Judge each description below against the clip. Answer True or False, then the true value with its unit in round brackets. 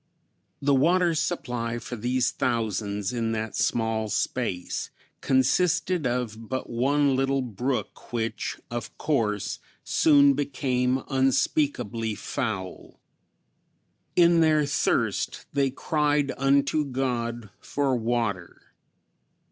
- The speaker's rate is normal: False (100 wpm)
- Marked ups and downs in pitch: False (3.7 semitones)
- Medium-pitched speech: False (125 Hz)